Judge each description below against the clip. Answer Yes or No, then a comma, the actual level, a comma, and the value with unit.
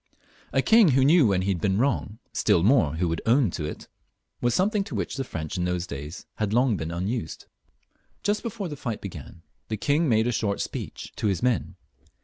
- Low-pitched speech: Yes, low, 110 Hz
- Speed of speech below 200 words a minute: No, fast, 205 wpm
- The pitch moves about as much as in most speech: No, wide, 7.2 semitones